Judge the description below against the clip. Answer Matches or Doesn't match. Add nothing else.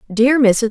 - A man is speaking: Doesn't match